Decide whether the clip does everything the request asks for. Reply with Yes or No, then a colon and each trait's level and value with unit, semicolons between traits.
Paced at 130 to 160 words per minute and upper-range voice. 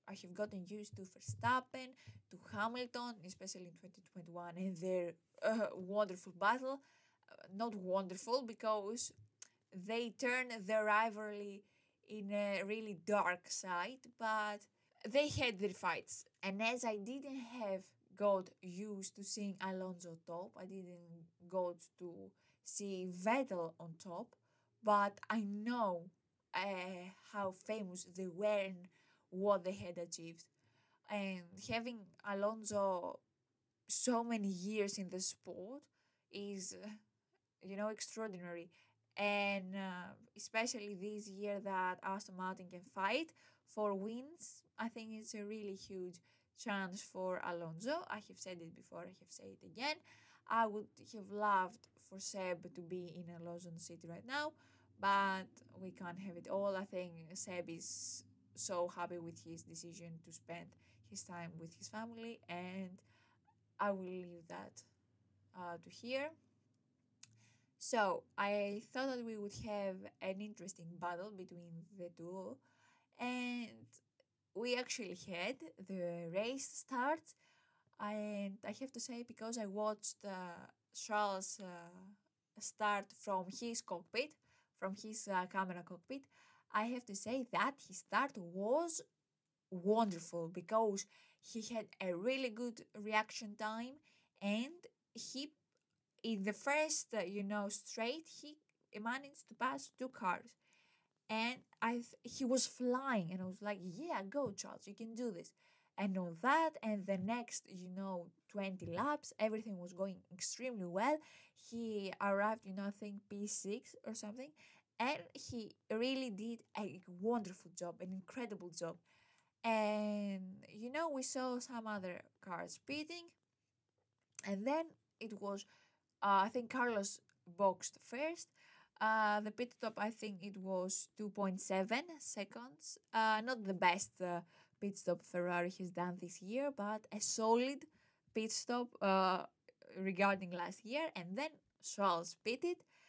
Yes: average, 140 wpm; high, 200 Hz